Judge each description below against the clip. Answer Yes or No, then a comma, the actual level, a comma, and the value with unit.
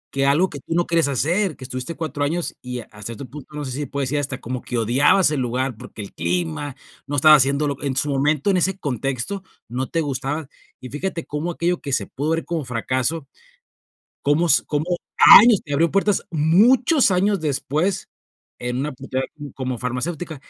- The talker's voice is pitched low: No, medium, 145 Hz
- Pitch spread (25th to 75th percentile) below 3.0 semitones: No, average, 4.3 semitones